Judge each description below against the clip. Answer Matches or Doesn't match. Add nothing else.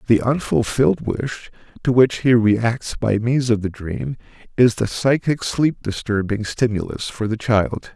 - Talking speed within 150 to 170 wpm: Matches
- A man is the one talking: Matches